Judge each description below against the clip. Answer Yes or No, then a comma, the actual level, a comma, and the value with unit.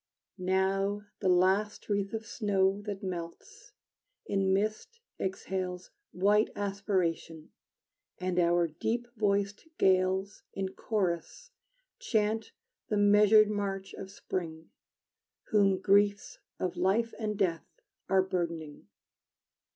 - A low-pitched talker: No, high, 195 Hz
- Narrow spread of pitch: Yes, narrow, 2.1 semitones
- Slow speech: Yes, slow, 105 wpm